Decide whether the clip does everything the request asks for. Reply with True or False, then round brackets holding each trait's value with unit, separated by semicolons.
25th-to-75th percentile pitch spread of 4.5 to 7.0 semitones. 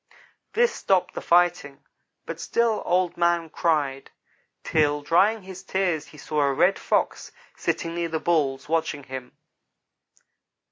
False (3.7 semitones)